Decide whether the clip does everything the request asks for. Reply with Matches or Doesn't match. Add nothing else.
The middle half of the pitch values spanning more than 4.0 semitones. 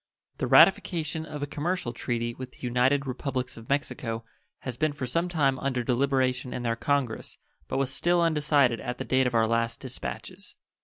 Doesn't match